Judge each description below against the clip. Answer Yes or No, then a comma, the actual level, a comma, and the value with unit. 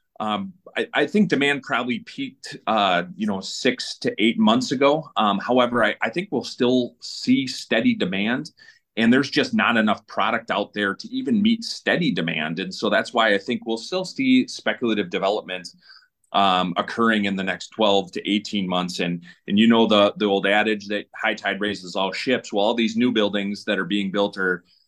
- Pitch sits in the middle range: No, low, 110 Hz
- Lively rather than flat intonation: Yes, wide, 7.2 semitones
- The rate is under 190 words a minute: No, average, 200 wpm